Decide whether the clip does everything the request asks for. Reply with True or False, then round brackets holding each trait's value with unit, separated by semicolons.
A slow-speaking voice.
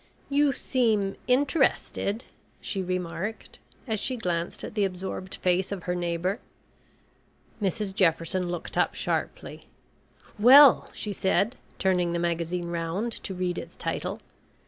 True (125 wpm)